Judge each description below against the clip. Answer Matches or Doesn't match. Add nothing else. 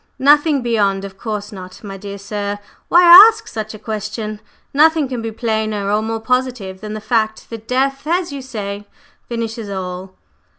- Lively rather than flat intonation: Doesn't match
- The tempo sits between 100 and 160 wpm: Doesn't match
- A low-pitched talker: Doesn't match